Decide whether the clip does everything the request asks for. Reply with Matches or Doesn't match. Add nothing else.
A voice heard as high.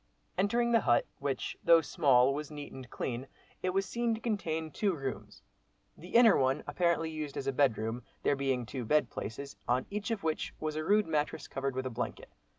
Doesn't match